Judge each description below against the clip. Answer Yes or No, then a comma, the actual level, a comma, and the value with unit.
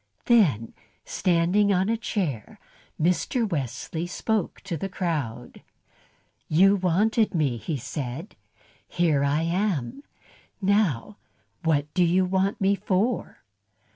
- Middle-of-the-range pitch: Yes, medium, 180 Hz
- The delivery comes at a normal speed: No, slow, 110 wpm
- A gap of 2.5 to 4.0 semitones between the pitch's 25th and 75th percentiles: No, average, 5.0 semitones